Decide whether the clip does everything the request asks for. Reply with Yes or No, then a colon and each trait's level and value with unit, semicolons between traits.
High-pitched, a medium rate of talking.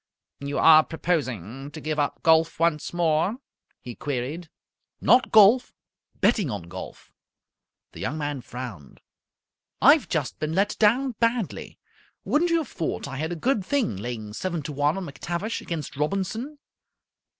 No: medium, 160 Hz; average, 150 wpm